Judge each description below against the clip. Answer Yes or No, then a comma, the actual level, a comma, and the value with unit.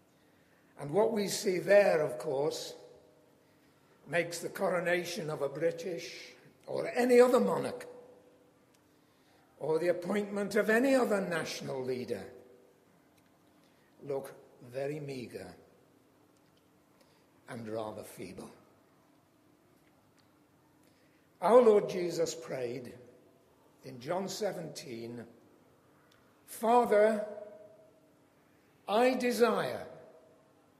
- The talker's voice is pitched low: No, medium, 175 Hz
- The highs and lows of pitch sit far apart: Yes, wide, 6.2 semitones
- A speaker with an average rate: No, slow, 80 wpm